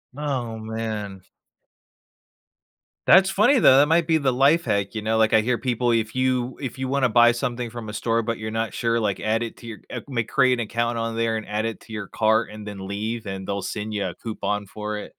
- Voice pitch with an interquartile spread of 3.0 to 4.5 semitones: No, narrow, 2.6 semitones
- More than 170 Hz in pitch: No, low, 115 Hz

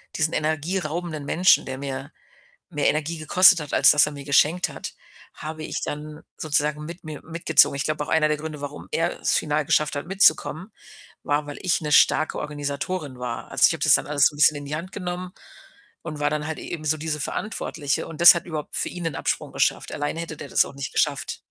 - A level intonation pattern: Yes, narrow, 2.1 semitones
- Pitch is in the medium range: Yes, medium, 155 Hz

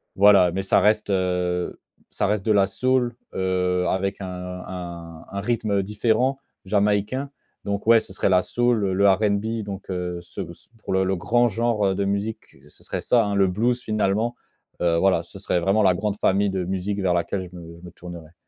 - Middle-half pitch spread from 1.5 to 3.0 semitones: Yes, average, 2.7 semitones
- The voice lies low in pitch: Yes, low, 100 Hz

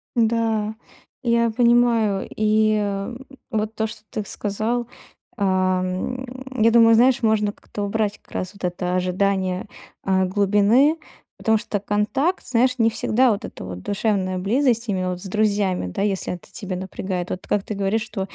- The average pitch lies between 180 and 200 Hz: No, high, 210 Hz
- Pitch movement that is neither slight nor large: Yes, average, 3.1 semitones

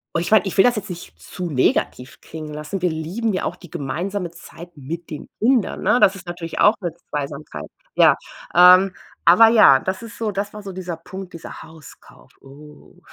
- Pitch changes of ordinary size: Yes, average, 3.8 semitones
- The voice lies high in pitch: No, medium, 175 Hz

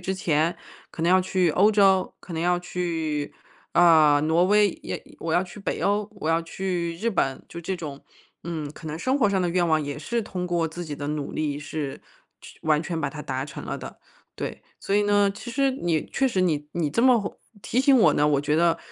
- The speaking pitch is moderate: Yes, medium, 170 Hz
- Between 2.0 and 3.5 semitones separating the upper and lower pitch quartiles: No, average, 3.9 semitones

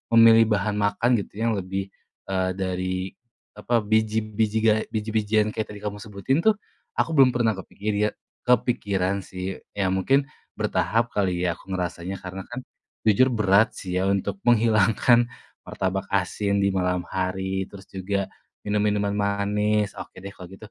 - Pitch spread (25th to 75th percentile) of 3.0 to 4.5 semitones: No, narrow, 2.5 semitones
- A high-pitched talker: No, low, 100 Hz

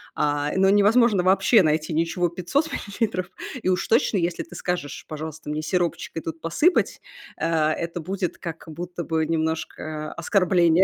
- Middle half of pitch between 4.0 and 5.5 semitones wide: No, average, 3.1 semitones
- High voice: No, medium, 170 Hz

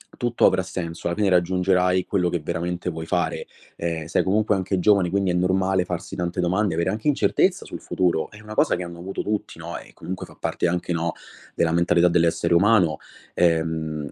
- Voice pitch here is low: Yes, very low, 90 Hz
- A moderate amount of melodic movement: No, narrow, 2.0 semitones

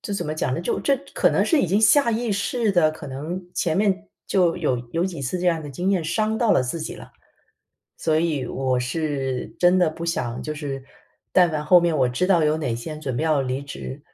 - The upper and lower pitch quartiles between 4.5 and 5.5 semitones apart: Yes, average, 4.8 semitones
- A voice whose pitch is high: No, medium, 160 Hz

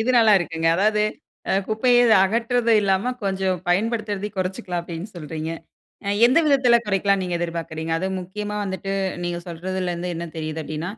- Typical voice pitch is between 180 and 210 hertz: Yes, high, 190 Hz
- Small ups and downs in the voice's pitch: No, average, 3.8 semitones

